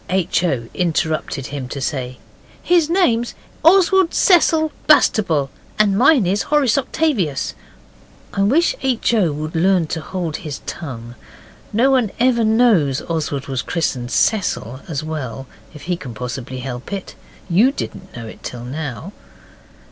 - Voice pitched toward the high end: No, medium, 175 Hz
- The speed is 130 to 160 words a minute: Yes, average, 145 wpm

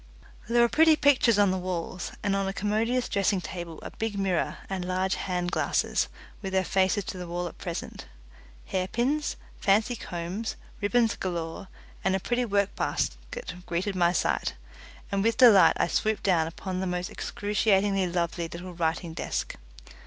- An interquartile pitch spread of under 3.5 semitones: Yes, average, 3.1 semitones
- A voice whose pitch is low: No, high, 190 Hz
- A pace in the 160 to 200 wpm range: Yes, average, 165 wpm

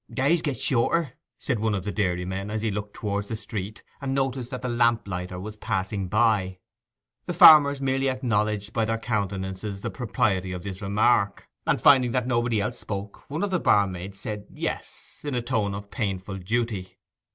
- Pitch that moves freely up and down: No, average, 3.9 semitones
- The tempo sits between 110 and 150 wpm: No, average, 185 wpm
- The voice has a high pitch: No, low, 105 Hz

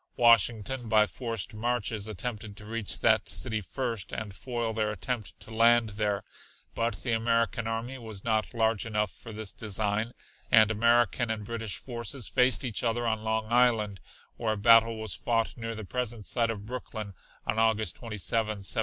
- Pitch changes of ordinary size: No, narrow, 1.7 semitones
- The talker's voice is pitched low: Yes, low, 110 Hz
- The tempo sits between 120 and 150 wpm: No, average, 170 wpm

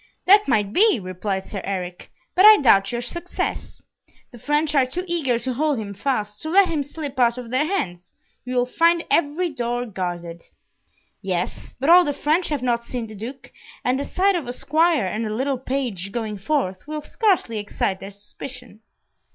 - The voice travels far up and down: Yes, wide, 6.7 semitones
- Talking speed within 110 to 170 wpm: No, average, 190 wpm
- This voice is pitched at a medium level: No, very high, 250 Hz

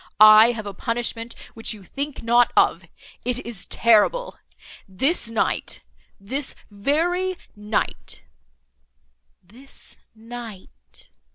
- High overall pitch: Yes, high, 230 Hz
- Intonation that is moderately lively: Yes, average, 3.9 semitones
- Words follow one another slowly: Yes, slow, 95 wpm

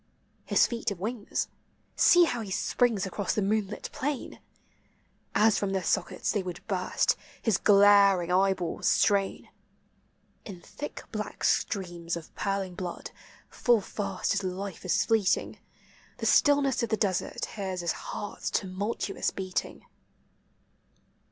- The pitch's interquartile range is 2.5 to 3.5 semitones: Yes, average, 2.8 semitones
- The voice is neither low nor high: No, high, 200 Hz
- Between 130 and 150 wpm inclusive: Yes, slow, 135 wpm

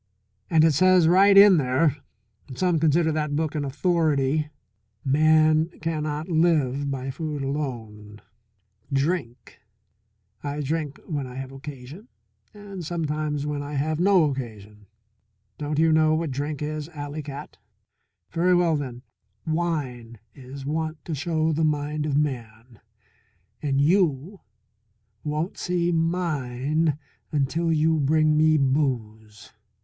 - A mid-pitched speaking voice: Yes, medium, 150 Hz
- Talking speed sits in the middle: No, slow, 125 wpm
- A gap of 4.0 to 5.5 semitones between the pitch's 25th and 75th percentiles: No, average, 3.0 semitones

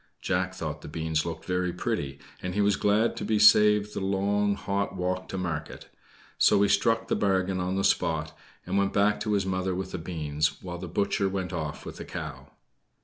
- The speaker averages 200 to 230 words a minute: Yes, fast, 205 wpm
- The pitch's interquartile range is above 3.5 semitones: No, average, 2.9 semitones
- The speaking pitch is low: Yes, very low, 95 Hz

